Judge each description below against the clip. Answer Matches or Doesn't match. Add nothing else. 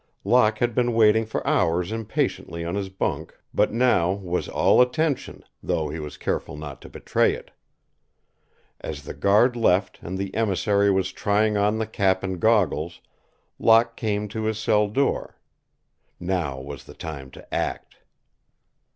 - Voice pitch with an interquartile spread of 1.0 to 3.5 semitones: Doesn't match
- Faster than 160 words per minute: Doesn't match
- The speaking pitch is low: Matches